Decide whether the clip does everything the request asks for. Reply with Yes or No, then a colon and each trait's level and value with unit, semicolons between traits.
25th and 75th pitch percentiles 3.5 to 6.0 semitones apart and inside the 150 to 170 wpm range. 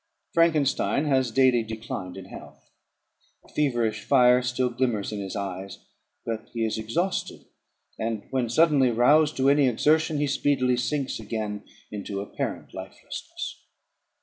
No: average, 4.2 semitones; slow, 135 wpm